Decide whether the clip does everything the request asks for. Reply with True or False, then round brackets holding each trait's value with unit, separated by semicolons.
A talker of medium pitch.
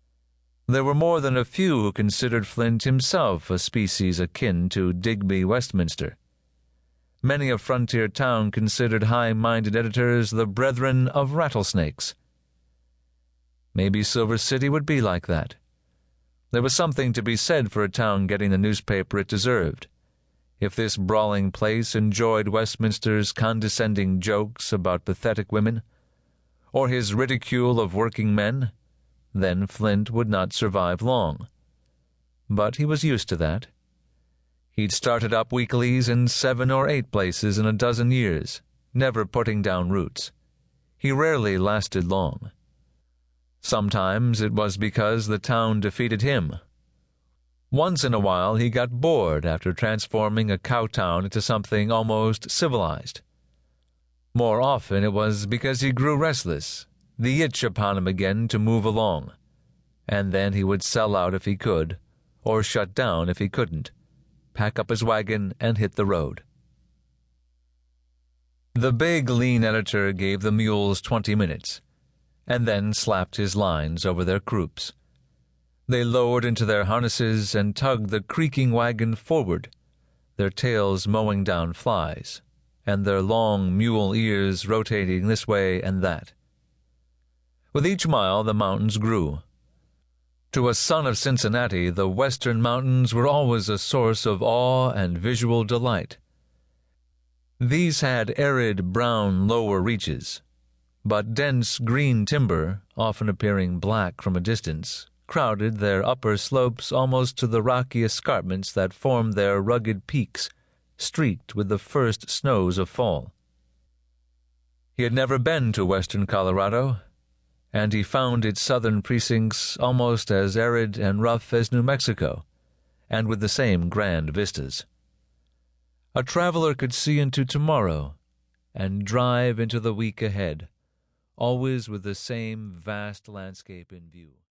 False (105 Hz)